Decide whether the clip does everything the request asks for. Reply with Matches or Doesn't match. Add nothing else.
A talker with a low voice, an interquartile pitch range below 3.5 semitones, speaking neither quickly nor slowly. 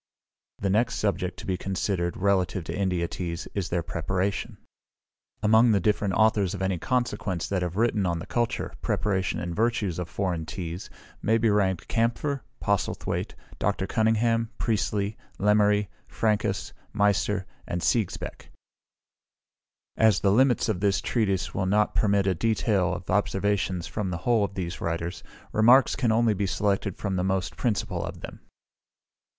Matches